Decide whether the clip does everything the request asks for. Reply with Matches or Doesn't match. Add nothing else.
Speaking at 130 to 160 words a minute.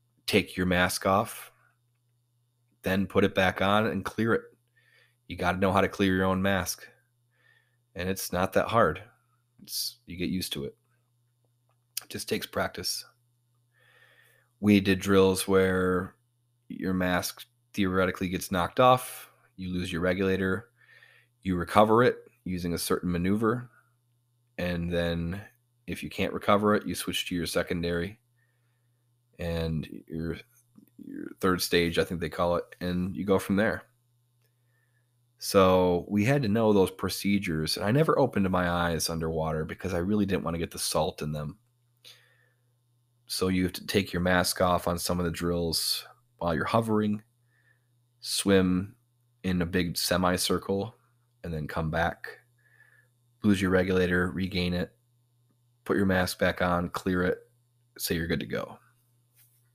Matches